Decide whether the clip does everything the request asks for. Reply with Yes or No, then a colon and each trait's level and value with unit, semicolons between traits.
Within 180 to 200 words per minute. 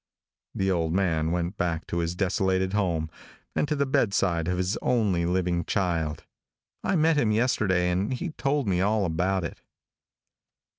No: average, 160 wpm